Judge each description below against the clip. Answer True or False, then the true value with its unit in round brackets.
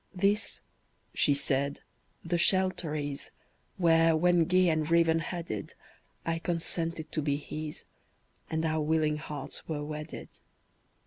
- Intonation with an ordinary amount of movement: False (1.9 semitones)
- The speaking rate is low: True (125 wpm)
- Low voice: False (160 Hz)